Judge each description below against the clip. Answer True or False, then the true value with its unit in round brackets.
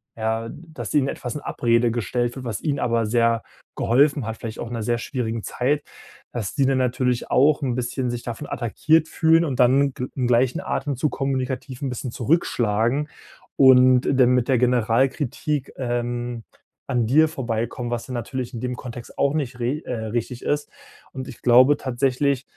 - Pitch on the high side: False (125 Hz)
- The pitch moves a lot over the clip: False (2.6 semitones)